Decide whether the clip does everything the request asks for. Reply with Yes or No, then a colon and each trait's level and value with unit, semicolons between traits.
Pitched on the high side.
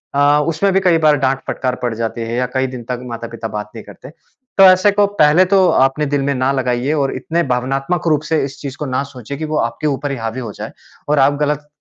No: low, 135 Hz